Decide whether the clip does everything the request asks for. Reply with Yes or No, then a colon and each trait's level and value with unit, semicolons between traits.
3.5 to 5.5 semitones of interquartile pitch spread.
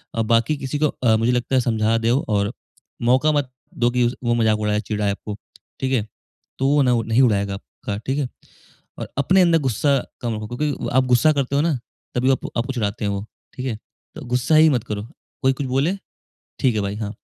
Yes: average, 3.8 semitones